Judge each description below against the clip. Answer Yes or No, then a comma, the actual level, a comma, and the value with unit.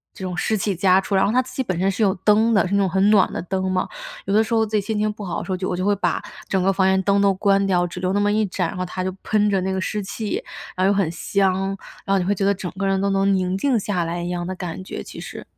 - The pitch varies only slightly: Yes, narrow, 1.8 semitones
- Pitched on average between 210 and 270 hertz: No, high, 195 Hz